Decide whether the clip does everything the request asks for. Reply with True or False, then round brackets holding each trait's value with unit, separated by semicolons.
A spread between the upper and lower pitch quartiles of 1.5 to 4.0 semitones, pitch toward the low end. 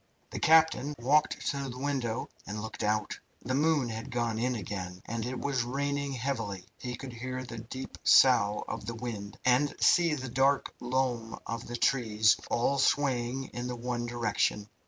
True (2.9 semitones; 125 Hz)